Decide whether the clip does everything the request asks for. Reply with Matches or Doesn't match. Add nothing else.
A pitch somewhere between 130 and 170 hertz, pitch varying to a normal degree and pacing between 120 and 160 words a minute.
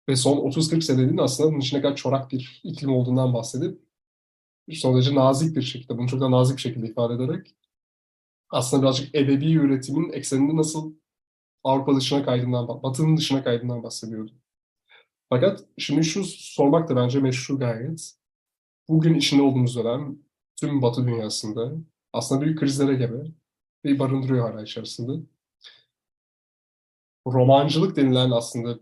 Matches